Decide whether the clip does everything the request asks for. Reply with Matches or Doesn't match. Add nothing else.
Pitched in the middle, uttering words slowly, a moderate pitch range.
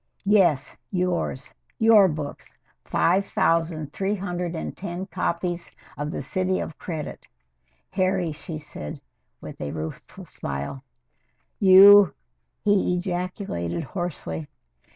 Matches